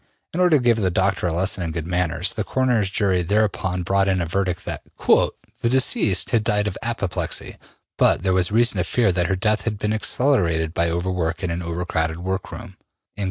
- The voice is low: Yes, very low, 95 Hz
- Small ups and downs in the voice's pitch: No, average, 3.6 semitones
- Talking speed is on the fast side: Yes, fast, 215 wpm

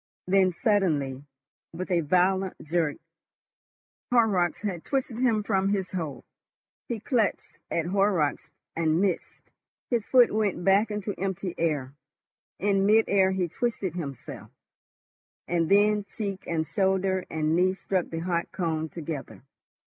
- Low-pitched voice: No, medium, 185 Hz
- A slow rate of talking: Yes, slow, 130 wpm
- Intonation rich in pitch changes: No, average, 3.5 semitones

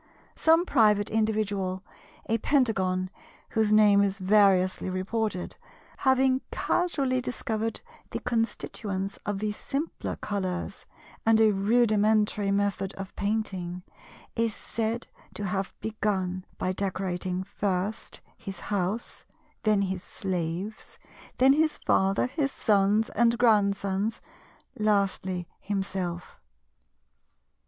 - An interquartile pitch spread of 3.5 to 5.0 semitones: No, average, 2.7 semitones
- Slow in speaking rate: Yes, slow, 100 wpm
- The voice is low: No, high, 205 Hz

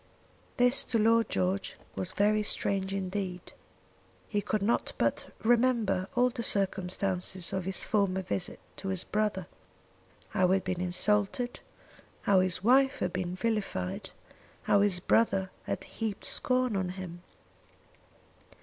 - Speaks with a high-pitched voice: Yes, high, 195 Hz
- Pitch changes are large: No, average, 3.0 semitones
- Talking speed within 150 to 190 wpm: No, slow, 135 wpm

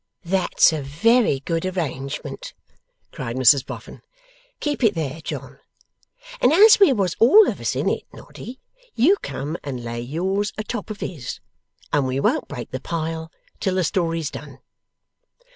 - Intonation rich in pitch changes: Yes, wide, 7.3 semitones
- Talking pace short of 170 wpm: Yes, average, 160 wpm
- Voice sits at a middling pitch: Yes, medium, 165 Hz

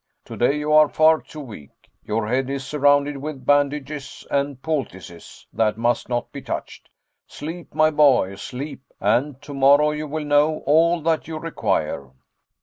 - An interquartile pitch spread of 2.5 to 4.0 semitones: Yes, average, 3.4 semitones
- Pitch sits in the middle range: Yes, medium, 145 Hz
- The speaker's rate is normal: Yes, average, 150 wpm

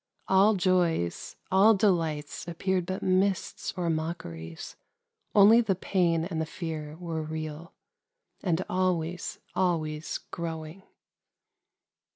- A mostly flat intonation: No, average, 3.0 semitones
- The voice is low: No, medium, 170 Hz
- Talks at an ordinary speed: No, slow, 115 wpm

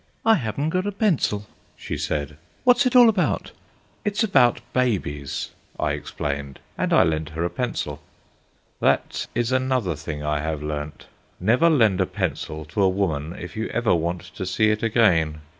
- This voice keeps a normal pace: Yes, average, 170 wpm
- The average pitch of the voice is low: Yes, very low, 95 Hz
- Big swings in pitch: Yes, wide, 8.8 semitones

